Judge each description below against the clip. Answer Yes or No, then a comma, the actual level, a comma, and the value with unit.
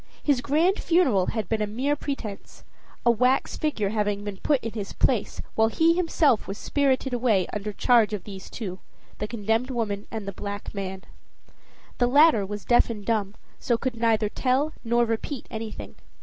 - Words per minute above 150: Yes, average, 180 wpm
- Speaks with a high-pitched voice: Yes, high, 225 Hz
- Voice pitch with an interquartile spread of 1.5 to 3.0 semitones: No, average, 4.0 semitones